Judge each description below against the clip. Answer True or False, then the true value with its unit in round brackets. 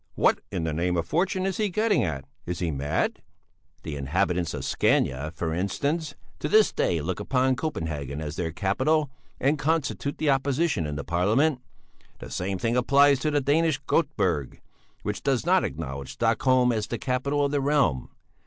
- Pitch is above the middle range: False (120 Hz)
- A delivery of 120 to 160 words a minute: False (170 wpm)